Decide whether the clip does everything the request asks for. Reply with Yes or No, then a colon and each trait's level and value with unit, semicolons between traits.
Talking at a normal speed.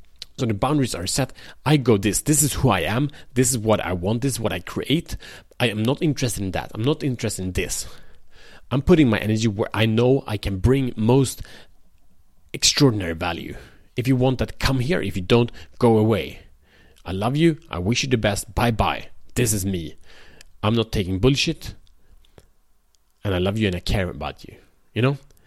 No: fast, 205 wpm